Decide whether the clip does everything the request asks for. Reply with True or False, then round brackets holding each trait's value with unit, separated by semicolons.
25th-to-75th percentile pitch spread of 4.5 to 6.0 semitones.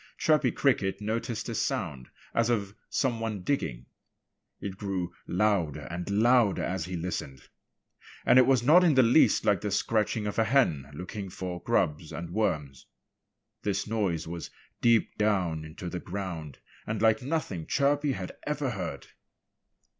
True (5.1 semitones)